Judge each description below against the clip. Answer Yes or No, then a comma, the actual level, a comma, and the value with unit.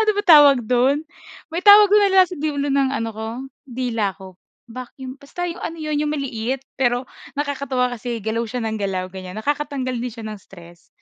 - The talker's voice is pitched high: Yes, very high, 255 Hz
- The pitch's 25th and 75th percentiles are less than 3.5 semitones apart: No, average, 4.6 semitones